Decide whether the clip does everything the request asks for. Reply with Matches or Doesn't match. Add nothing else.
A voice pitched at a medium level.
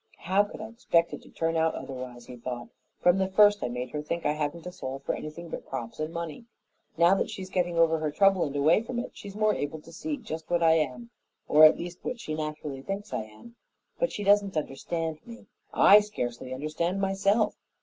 Matches